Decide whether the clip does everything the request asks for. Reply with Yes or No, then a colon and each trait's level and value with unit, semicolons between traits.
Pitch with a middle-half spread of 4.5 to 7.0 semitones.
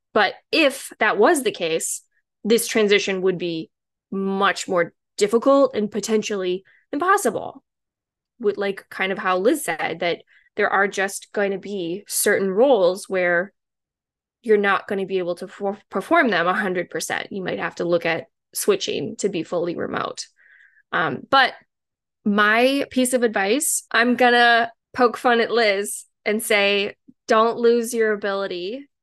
No: average, 3.4 semitones